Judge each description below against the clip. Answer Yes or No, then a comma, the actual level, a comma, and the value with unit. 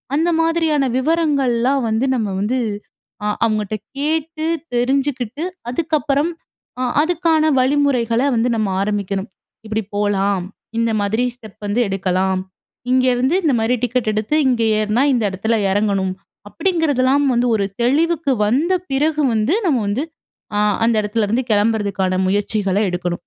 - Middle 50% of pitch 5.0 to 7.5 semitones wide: Yes, wide, 5.6 semitones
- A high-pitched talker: Yes, high, 240 Hz